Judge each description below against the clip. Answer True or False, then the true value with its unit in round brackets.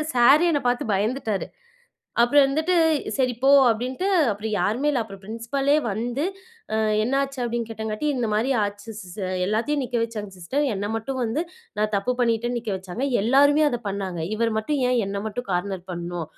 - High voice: True (230 Hz)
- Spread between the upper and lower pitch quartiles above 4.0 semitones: True (4.5 semitones)